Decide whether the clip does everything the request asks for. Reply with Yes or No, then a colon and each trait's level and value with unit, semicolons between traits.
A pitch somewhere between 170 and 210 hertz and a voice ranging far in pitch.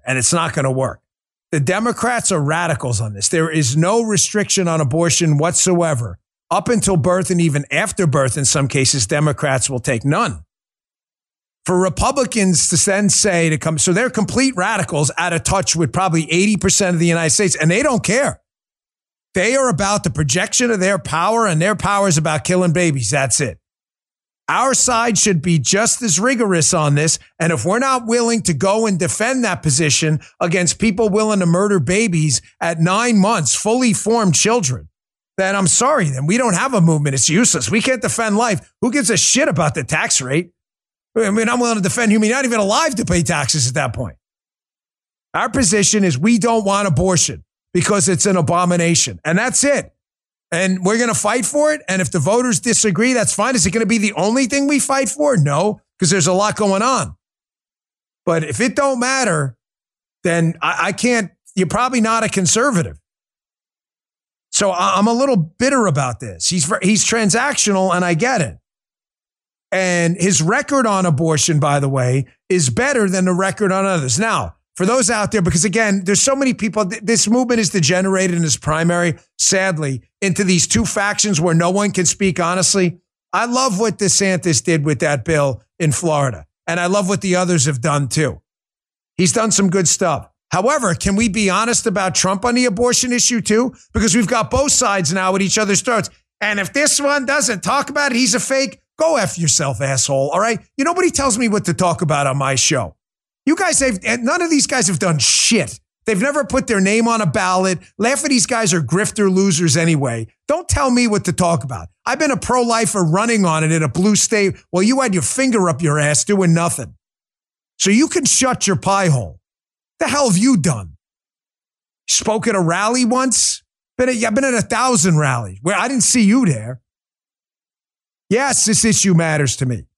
Yes: high, 190 Hz; wide, 5.7 semitones